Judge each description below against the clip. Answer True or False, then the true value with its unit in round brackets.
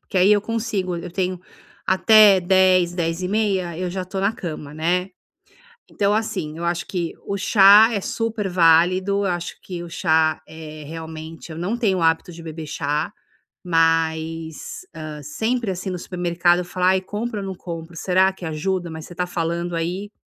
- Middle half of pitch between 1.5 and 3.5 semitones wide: True (2.8 semitones)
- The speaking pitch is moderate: True (180 Hz)